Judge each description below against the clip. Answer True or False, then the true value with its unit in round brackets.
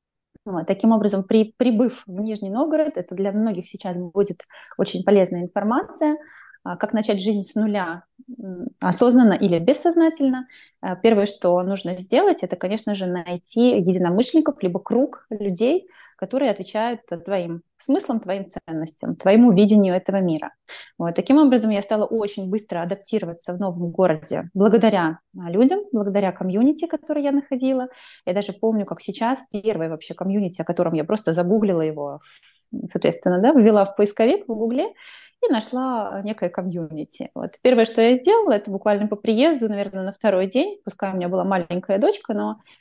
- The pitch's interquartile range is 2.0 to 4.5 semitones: False (4.9 semitones)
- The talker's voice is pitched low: False (210 Hz)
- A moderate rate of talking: True (150 wpm)